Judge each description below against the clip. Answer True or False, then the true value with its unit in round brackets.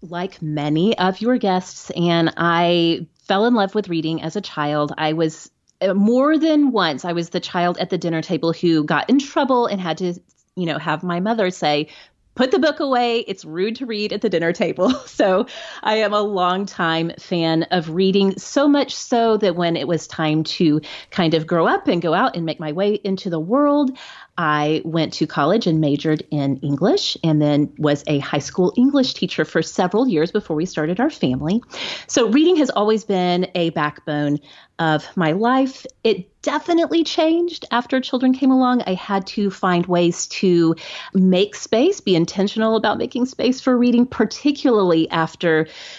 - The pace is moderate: True (185 wpm)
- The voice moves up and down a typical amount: False (6.2 semitones)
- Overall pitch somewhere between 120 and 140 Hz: False (185 Hz)